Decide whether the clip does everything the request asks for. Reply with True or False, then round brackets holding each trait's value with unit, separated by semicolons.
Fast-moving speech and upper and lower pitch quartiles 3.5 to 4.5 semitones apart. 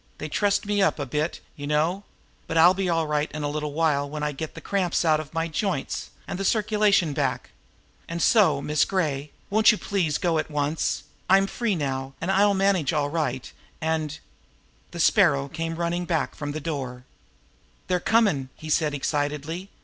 False (190 wpm; 4.2 semitones)